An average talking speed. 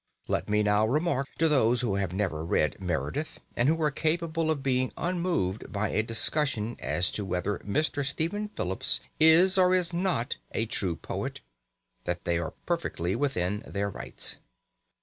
Yes: average, 165 wpm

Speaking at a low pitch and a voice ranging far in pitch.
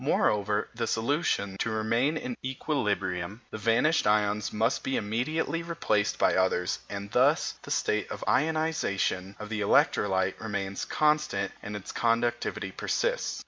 Yes: low, 110 Hz; wide, 5.7 semitones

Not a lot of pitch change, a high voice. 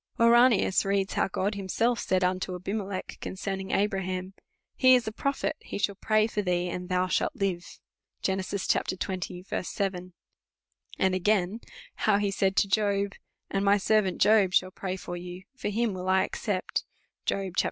Yes: narrow, 1.9 semitones; high, 195 Hz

